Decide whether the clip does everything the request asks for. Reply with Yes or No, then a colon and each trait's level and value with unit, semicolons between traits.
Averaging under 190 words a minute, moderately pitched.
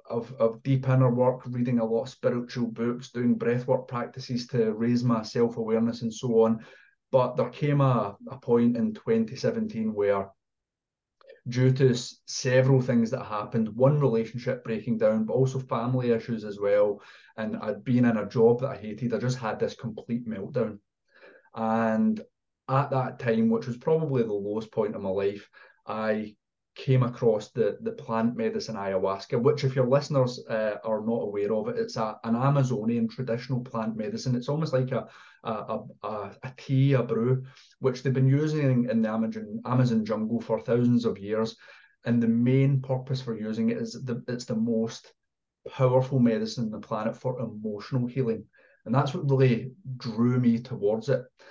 No: average, 175 wpm; low, 120 Hz